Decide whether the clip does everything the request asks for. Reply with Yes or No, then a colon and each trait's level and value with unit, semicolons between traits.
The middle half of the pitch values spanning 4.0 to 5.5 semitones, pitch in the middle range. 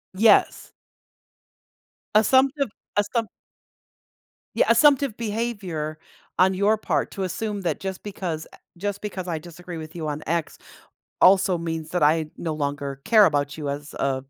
Yes: average, 5.0 semitones; medium, 180 Hz